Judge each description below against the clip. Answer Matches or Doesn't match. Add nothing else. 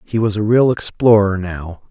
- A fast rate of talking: Doesn't match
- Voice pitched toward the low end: Matches